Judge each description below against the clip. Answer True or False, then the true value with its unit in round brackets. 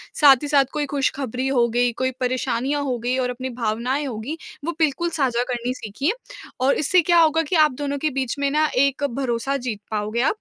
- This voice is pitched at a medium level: False (265 Hz)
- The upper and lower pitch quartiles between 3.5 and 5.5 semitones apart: False (3.0 semitones)